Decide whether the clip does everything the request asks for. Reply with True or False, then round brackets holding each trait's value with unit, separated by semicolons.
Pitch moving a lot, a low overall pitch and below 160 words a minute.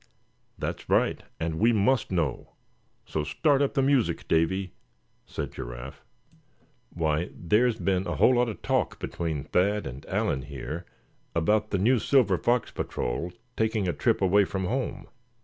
True (6.1 semitones; 95 Hz; 150 wpm)